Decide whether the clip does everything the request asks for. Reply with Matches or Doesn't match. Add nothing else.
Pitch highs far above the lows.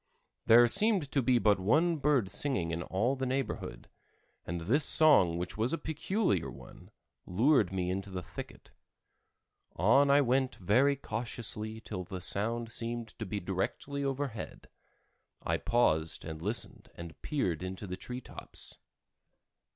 Matches